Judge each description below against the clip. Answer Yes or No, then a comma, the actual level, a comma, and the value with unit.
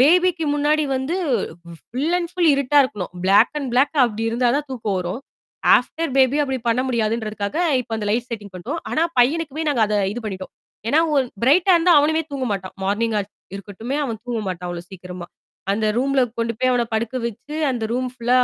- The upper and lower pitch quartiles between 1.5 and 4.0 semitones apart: No, average, 5.2 semitones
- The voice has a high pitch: Yes, high, 245 Hz